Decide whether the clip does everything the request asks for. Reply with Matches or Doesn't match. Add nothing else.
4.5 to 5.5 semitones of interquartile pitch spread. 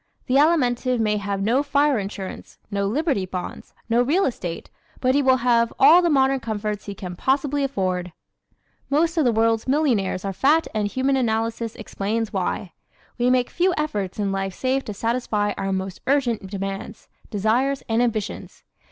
Matches